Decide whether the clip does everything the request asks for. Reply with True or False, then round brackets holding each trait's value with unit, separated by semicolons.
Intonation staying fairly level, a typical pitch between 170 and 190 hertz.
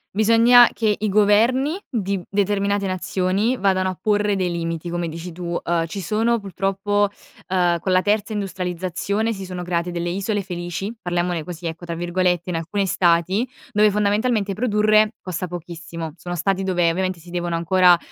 False (3.0 semitones; 185 Hz)